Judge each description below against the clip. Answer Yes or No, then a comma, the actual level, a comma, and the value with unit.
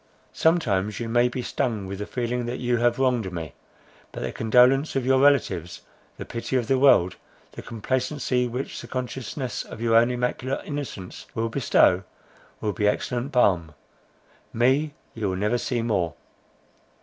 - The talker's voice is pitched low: Yes, low, 120 Hz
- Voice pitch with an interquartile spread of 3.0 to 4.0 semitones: Yes, average, 3.6 semitones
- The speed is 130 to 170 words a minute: Yes, average, 160 wpm